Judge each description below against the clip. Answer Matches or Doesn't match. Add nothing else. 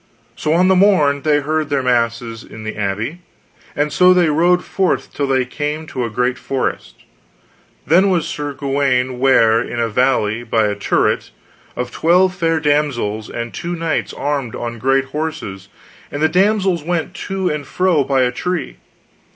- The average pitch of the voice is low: Doesn't match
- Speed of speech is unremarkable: Matches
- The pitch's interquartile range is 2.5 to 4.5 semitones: Doesn't match